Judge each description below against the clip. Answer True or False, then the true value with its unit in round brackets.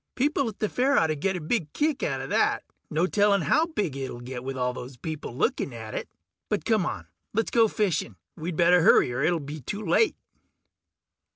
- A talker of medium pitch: True (170 Hz)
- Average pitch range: False (7.7 semitones)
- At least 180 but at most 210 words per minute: True (200 wpm)